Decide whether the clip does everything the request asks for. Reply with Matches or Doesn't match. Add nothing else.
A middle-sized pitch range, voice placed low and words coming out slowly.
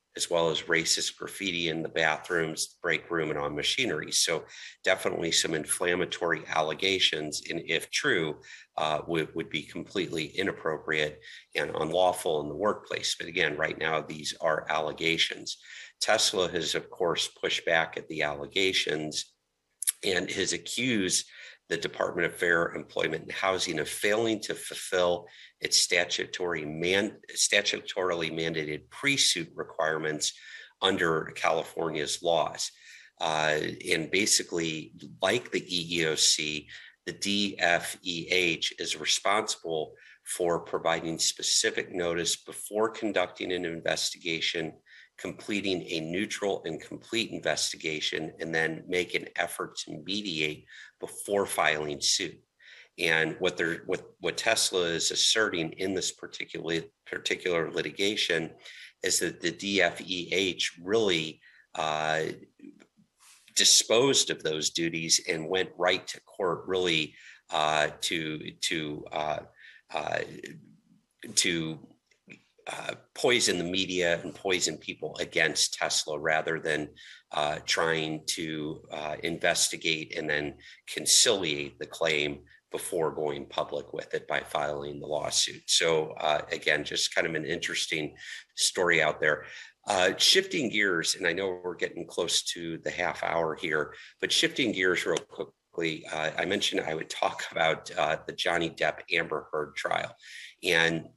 Matches